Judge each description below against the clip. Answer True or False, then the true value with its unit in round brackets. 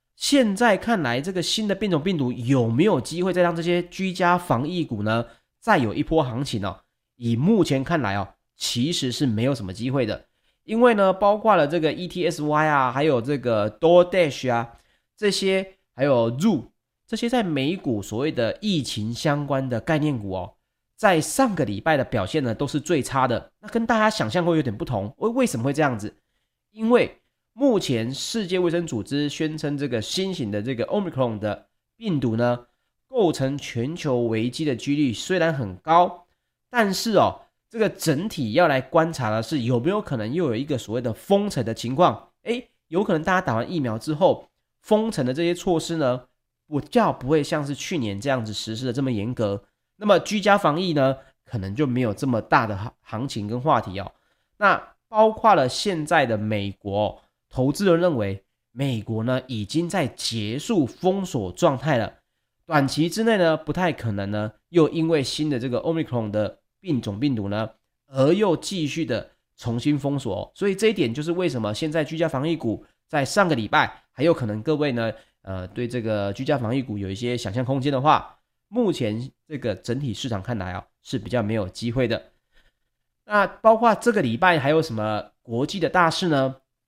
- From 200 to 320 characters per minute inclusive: True (290 characters per minute)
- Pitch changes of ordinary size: False (6.8 semitones)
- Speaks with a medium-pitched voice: True (145 Hz)